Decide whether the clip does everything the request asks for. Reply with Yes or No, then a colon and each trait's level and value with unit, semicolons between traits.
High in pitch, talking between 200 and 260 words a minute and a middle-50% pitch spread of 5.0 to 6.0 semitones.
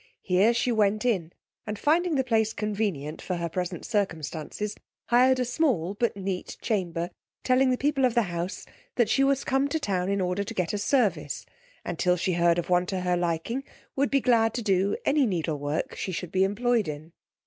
Yes: high, 200 Hz; fast, 205 wpm; wide, 5.4 semitones